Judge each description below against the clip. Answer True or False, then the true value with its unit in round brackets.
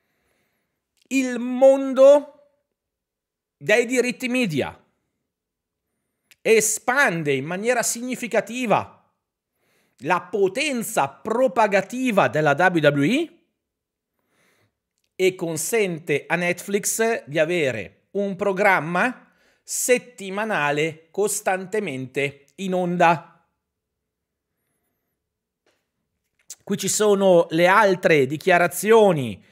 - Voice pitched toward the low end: False (200 Hz)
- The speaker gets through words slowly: True (65 wpm)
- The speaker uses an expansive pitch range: True (6.5 semitones)